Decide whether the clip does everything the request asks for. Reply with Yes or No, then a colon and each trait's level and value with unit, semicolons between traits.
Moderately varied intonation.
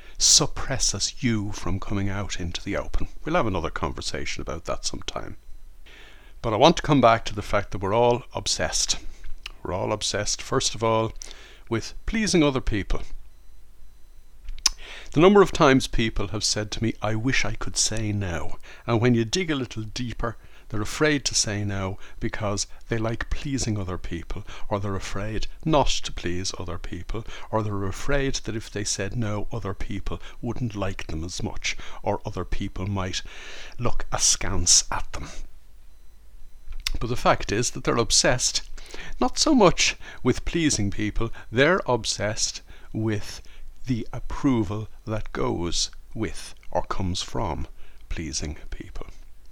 Yes: average, 4.4 semitones